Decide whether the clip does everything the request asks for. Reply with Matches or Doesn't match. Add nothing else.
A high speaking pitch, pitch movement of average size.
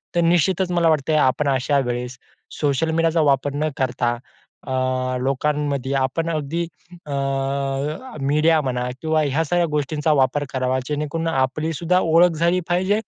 Doesn't match